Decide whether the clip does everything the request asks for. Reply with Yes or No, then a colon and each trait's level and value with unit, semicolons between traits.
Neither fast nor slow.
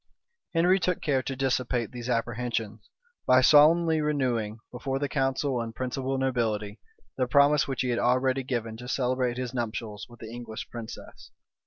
Yes: average, 160 wpm